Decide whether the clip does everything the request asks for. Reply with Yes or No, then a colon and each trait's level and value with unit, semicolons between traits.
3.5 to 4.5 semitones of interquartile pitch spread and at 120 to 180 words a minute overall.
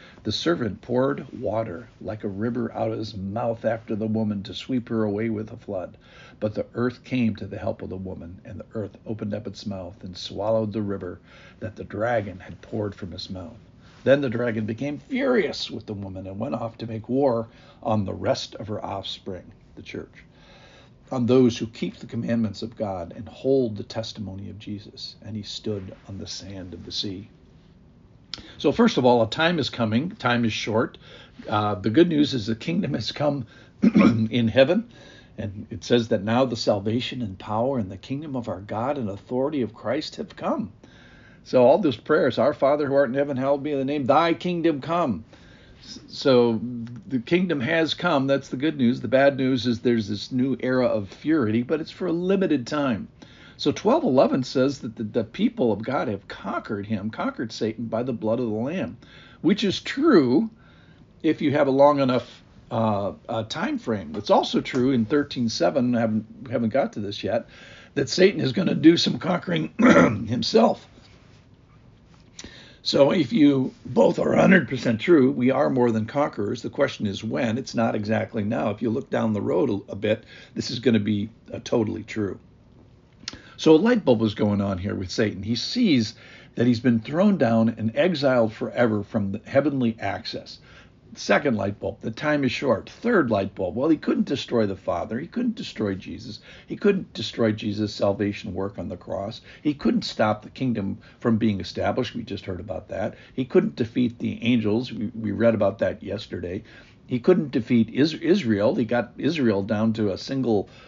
No: average, 3.9 semitones; average, 195 wpm